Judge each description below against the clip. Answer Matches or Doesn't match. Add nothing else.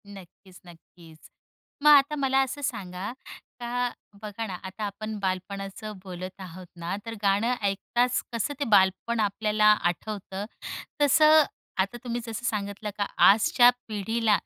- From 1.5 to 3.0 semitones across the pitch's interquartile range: Doesn't match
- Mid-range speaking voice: Doesn't match